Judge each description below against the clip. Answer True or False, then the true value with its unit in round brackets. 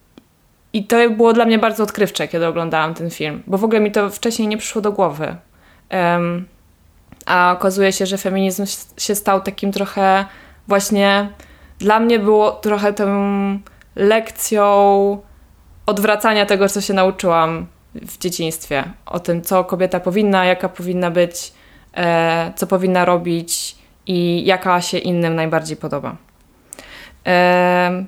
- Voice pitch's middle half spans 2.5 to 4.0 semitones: True (2.8 semitones)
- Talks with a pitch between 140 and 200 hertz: True (190 Hz)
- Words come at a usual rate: True (135 wpm)